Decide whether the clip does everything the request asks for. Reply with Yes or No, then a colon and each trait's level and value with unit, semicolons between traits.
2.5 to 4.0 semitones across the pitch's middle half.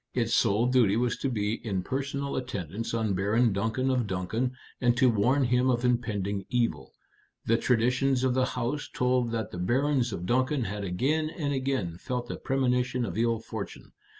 Yes: average, 3.4 semitones